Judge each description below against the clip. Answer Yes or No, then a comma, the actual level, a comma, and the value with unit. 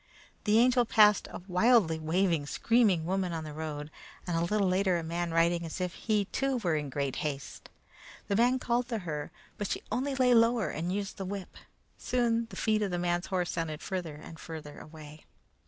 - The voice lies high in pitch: No, medium, 180 Hz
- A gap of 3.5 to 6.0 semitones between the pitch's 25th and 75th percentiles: Yes, average, 5.2 semitones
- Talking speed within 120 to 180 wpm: No, average, 200 wpm